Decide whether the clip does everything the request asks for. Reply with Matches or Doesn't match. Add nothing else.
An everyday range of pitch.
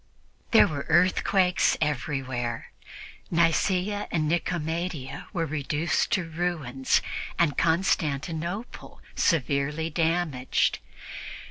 Matches